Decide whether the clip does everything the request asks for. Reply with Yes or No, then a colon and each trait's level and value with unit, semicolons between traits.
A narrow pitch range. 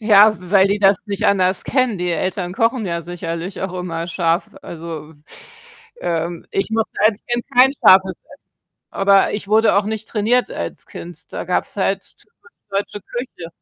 No: average, 3.8 semitones